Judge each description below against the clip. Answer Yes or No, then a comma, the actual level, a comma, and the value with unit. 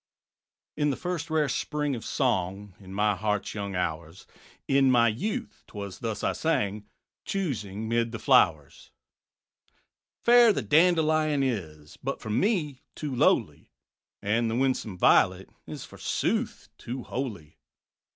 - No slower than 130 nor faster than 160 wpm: Yes, average, 140 wpm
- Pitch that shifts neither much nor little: No, wide, 6.7 semitones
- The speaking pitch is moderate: No, low, 115 Hz